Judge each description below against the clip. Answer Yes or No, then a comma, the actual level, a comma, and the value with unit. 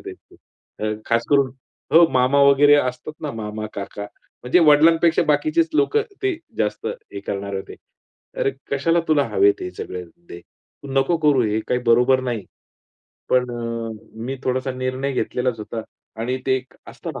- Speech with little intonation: No, average, 4.2 semitones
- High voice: No, low, 130 Hz